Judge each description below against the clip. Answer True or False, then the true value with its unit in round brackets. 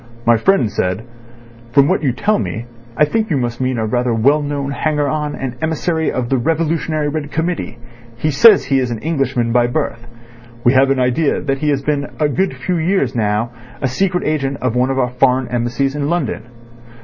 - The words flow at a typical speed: False (210 wpm)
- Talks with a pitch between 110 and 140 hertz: True (135 Hz)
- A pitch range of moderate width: True (4.0 semitones)